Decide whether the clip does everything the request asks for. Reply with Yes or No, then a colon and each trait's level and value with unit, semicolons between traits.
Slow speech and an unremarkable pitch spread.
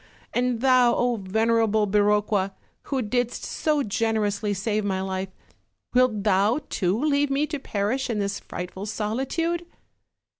Yes: slow, 125 wpm; average, 3.8 semitones